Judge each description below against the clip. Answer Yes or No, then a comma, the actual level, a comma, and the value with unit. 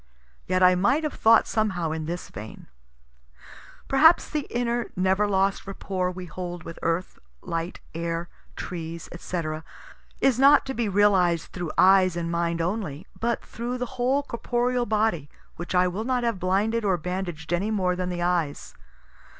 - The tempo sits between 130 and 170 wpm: Yes, average, 160 wpm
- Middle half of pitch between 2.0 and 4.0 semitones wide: No, average, 4.9 semitones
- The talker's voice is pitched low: No, medium, 185 Hz